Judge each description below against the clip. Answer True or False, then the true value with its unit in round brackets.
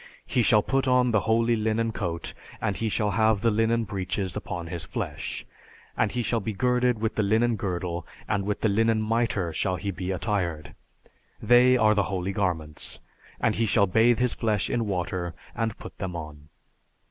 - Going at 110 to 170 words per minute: False (185 wpm)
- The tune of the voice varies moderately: True (3.8 semitones)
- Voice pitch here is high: False (105 Hz)